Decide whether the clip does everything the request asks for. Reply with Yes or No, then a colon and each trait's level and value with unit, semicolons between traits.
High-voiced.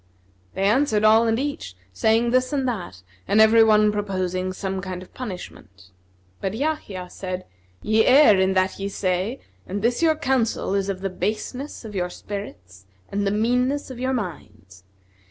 Yes: high, 205 Hz